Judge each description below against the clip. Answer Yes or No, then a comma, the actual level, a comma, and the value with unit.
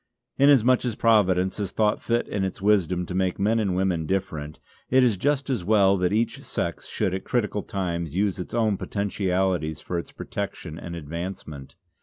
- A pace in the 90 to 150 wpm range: No, average, 180 wpm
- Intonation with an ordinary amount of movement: Yes, average, 3.3 semitones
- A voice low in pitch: Yes, very low, 95 Hz